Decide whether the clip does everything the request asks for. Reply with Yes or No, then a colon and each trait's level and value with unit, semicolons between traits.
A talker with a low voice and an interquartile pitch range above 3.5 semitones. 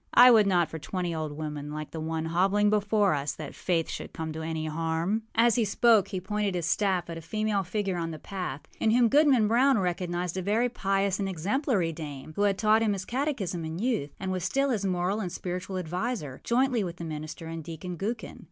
No: medium, 185 Hz; average, 4.7 semitones